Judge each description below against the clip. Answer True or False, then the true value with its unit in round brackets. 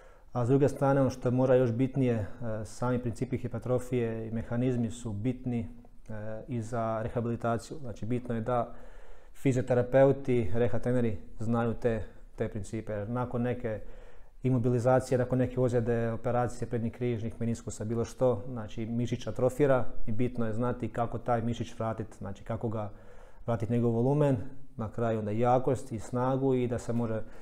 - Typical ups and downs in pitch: False (1.6 semitones)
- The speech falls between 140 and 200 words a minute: True (155 wpm)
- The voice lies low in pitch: True (120 Hz)